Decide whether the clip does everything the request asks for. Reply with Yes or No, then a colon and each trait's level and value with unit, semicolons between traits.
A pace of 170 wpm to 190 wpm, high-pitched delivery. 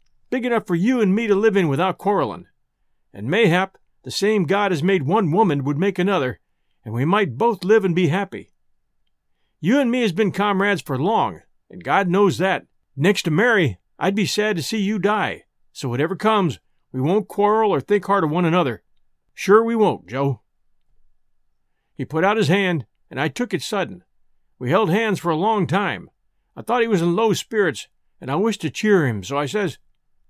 No: average, 200 wpm; high, 195 Hz